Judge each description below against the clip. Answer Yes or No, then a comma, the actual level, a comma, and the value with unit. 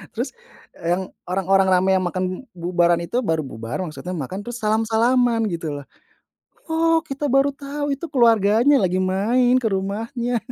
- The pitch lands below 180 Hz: No, high, 215 Hz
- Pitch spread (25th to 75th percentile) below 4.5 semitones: No, wide, 5.5 semitones